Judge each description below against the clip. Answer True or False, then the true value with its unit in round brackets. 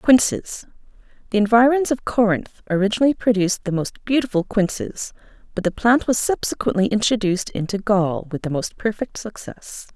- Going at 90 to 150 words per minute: True (140 wpm)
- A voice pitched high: True (210 Hz)